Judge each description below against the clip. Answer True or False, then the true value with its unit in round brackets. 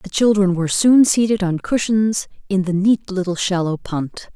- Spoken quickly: False (180 wpm)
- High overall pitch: True (195 Hz)